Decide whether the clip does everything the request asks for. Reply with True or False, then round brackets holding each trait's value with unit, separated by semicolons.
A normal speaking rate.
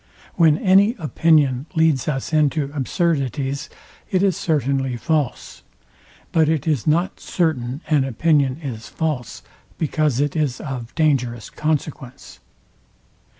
False (115 wpm)